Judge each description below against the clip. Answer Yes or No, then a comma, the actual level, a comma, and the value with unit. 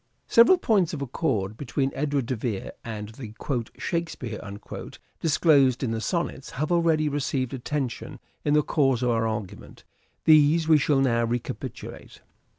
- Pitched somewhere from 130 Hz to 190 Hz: Yes, low, 135 Hz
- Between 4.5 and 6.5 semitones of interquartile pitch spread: Yes, average, 4.9 semitones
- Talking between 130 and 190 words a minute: Yes, average, 155 wpm